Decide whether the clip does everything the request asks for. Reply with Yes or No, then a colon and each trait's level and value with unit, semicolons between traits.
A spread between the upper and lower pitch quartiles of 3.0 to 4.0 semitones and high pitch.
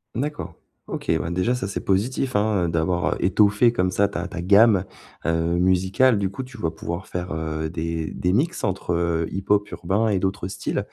No: average, 3.3 semitones; very low, 95 Hz